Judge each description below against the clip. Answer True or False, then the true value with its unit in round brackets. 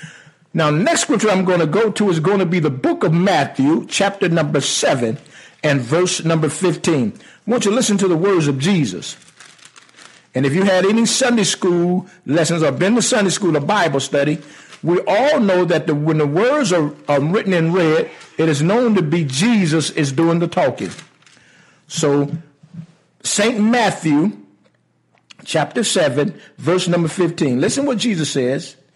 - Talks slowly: False (175 wpm)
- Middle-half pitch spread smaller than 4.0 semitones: False (4.4 semitones)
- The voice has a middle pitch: True (170 Hz)